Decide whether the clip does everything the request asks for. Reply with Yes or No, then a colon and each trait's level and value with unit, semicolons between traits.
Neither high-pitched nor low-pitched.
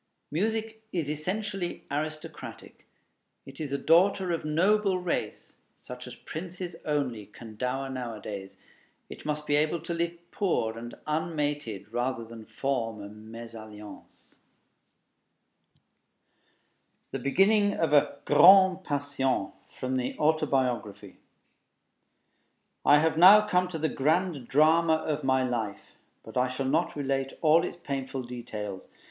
Yes: medium, 145 Hz